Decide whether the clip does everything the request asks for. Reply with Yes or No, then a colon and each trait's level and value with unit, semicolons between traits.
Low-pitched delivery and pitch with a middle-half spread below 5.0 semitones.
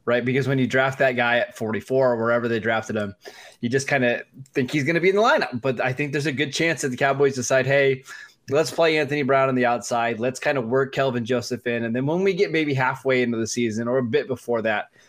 Yes: low, 130 Hz; average, 2.8 semitones